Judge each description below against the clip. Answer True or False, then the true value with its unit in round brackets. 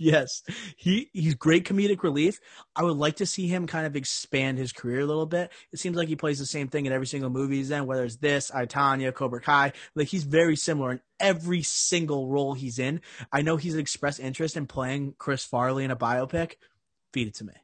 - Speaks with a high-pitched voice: False (145 Hz)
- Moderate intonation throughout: True (3.7 semitones)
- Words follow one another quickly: True (225 wpm)